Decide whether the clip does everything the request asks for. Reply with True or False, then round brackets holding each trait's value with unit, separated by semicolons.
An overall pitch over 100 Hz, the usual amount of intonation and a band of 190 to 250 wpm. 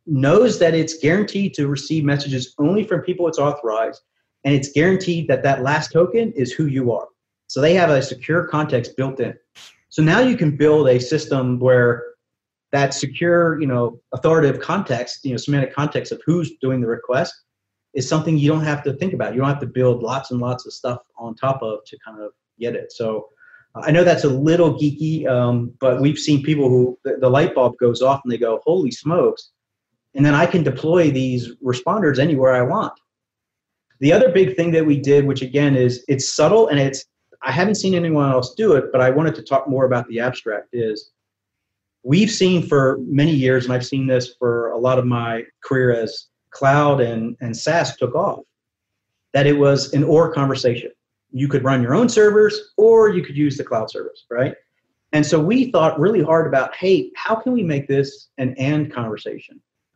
True (140 Hz; 4.3 semitones; 205 wpm)